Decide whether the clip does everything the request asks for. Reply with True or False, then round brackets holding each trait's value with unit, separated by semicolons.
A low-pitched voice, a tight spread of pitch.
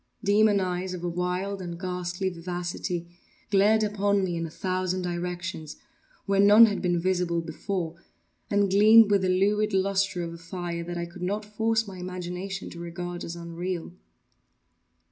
False (185 Hz; 2.3 semitones)